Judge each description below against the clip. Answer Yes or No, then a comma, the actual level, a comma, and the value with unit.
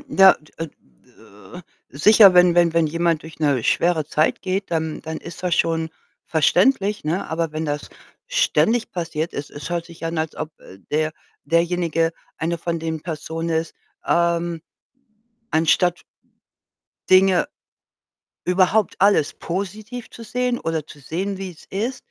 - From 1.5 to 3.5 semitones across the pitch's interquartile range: Yes, average, 2.8 semitones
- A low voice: No, medium, 170 Hz